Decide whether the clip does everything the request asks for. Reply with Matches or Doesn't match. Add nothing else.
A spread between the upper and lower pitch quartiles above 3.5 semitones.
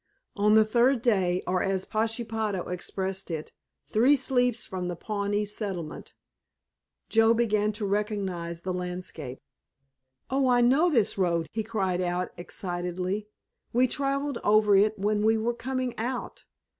Matches